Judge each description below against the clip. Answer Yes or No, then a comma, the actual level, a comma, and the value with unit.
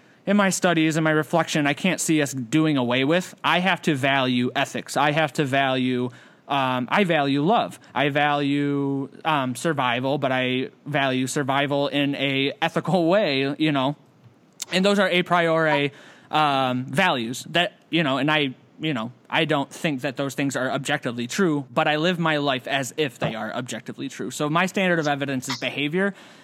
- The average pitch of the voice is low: No, medium, 145 Hz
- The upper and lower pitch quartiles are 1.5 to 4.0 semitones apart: Yes, average, 3.1 semitones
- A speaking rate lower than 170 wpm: No, average, 185 wpm